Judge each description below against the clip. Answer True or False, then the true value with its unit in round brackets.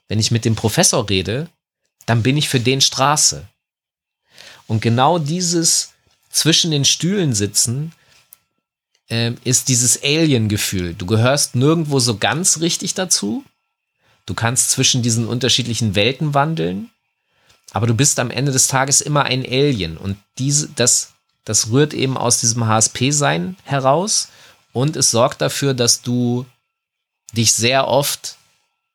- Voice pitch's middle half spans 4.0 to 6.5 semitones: True (4.3 semitones)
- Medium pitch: False (130 Hz)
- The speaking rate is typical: True (135 wpm)